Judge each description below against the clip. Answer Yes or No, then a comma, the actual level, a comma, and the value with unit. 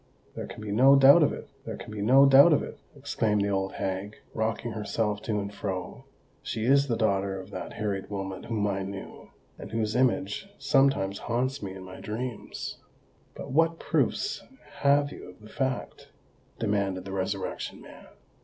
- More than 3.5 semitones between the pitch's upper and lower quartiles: Yes, average, 5.1 semitones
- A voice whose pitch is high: No, low, 105 Hz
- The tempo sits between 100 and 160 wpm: No, average, 175 wpm